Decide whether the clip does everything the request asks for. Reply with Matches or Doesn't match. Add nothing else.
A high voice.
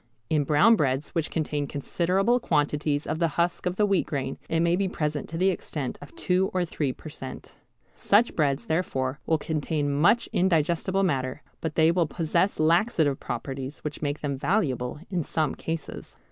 Doesn't match